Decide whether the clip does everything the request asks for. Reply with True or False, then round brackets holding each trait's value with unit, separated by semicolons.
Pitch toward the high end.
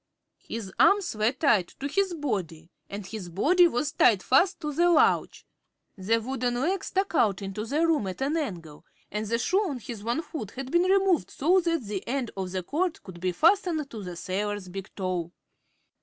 True (240 Hz)